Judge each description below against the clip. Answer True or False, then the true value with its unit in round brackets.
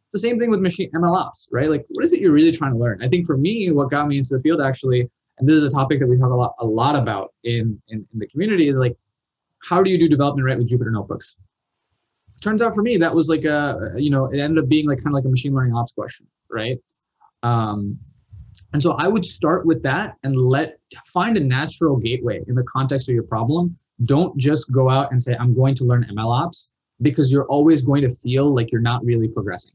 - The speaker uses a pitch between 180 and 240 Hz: False (135 Hz)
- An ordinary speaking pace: False (255 wpm)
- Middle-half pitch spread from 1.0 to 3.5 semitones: False (4.3 semitones)